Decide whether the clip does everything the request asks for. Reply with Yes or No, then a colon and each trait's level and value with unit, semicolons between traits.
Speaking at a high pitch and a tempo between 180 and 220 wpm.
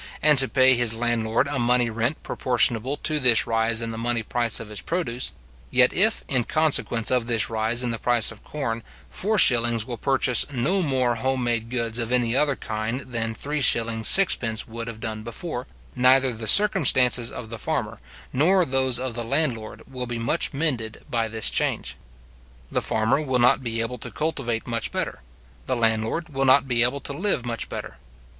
No: low, 120 Hz; average, 185 wpm